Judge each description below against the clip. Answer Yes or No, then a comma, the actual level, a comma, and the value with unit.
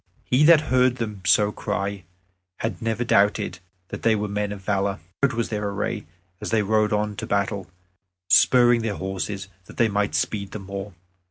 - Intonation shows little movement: Yes, narrow, 2.2 semitones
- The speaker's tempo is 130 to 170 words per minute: No, average, 180 wpm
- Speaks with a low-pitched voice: Yes, low, 105 Hz